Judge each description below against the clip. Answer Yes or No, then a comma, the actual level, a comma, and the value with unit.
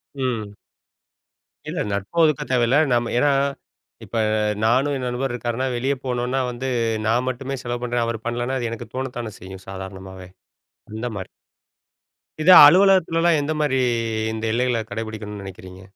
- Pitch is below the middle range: Yes, low, 120 Hz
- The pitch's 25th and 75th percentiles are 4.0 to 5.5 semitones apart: No, average, 3.3 semitones